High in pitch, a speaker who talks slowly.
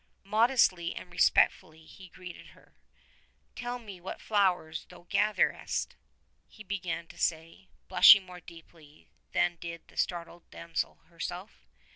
No: medium, 175 Hz; slow, 125 wpm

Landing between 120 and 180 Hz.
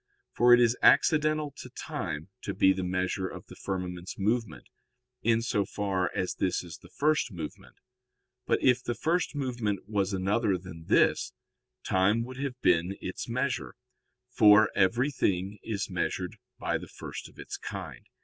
No: low, 105 Hz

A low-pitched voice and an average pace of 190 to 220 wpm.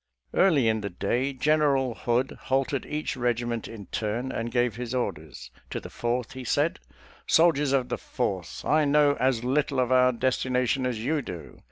Yes: low, 125 Hz; average, 195 wpm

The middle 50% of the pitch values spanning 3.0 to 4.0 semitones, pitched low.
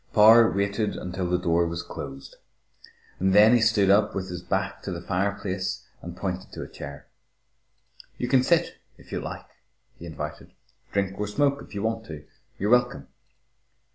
Yes: average, 3.5 semitones; low, 100 Hz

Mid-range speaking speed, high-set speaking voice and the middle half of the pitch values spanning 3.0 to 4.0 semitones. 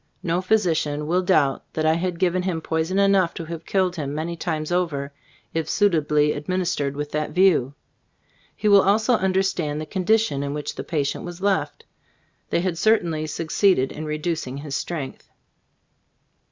No: average, 160 wpm; medium, 165 Hz; average, 3.7 semitones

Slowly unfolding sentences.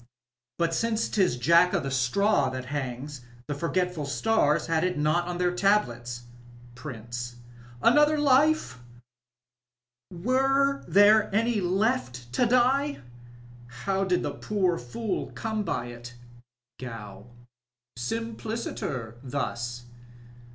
Yes: slow, 115 wpm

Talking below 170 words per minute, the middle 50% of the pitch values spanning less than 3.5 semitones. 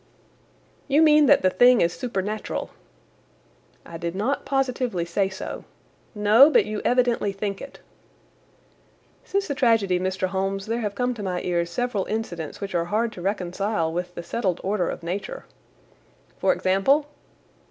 No: average, 150 wpm; average, 5.1 semitones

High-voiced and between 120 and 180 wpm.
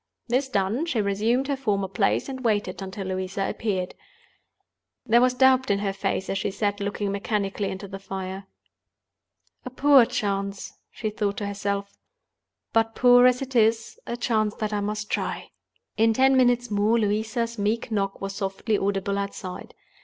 Yes: high, 210 Hz; average, 165 wpm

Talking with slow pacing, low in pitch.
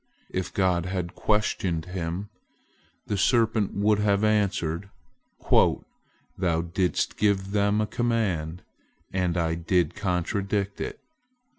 Yes: slow, 110 wpm; very low, 95 Hz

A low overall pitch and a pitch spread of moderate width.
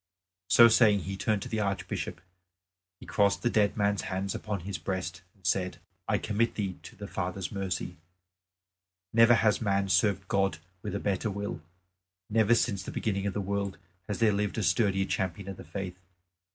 No: low, 100 Hz; narrow, 1.7 semitones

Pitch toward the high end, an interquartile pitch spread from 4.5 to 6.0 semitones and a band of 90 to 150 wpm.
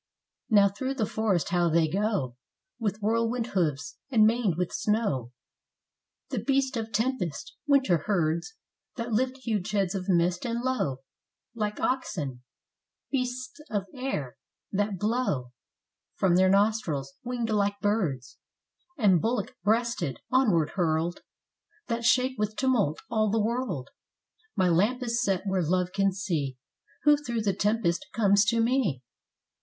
Yes: high, 205 Hz; average, 5.0 semitones; average, 140 wpm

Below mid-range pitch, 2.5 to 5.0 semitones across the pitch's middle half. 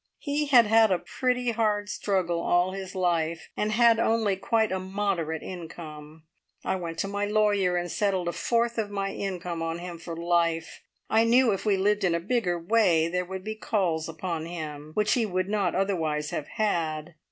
No: medium, 185 Hz; average, 4.0 semitones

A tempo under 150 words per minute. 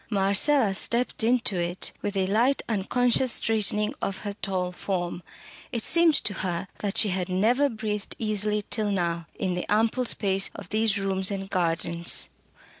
No: average, 160 wpm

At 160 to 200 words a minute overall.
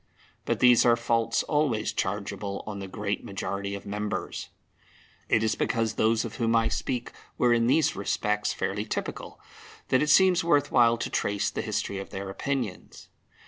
Yes: average, 170 wpm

